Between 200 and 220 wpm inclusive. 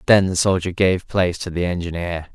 Yes: fast, 205 wpm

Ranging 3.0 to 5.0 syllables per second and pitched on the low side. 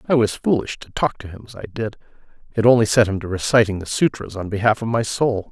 No: 6.1 syllables/s; low, 110 Hz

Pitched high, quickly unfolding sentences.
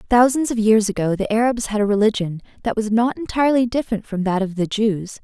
Yes: high, 220 Hz; fast, 220 wpm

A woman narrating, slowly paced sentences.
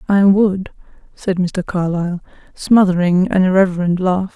Yes: female; slow, 125 wpm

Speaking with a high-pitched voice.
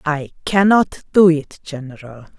No: medium, 160 Hz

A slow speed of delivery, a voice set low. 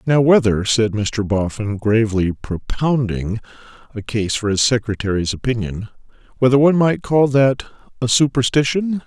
Yes: slow, 130 wpm; low, 120 Hz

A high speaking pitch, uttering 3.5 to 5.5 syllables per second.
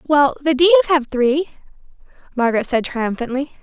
Yes: very high, 275 Hz; 5.4 syllables/s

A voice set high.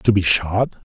No: very low, 95 Hz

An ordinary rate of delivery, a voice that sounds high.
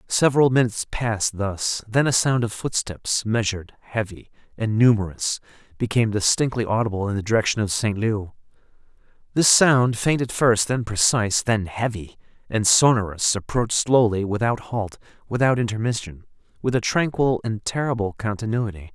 No: average, 145 wpm; low, 110 Hz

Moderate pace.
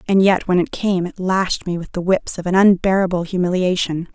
No: fast, 215 wpm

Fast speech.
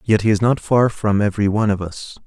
Yes: fast, 265 wpm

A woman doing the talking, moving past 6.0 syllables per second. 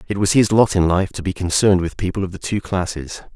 No: male; 6.2 syllables/s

